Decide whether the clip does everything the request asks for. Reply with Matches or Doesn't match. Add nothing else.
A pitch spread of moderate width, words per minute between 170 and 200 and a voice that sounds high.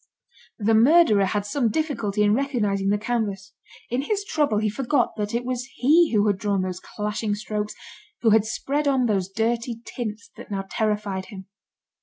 Matches